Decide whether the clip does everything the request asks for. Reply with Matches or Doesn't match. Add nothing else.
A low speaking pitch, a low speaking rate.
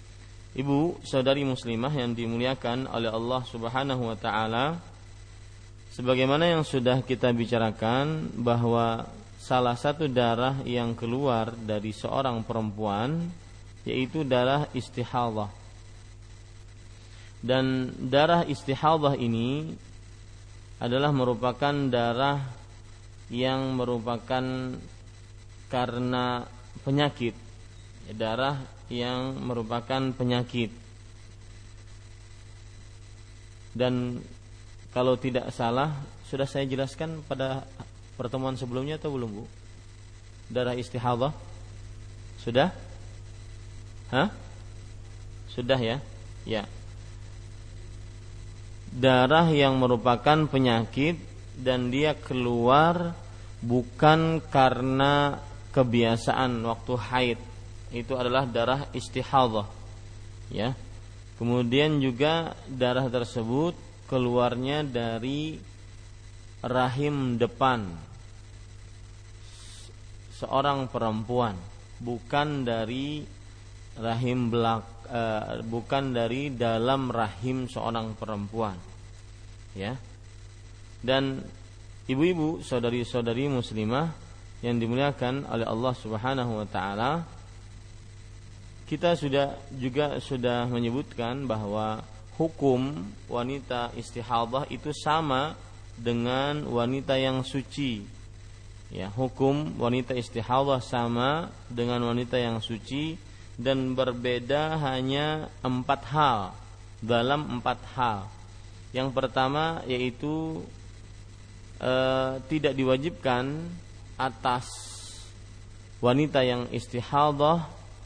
Matches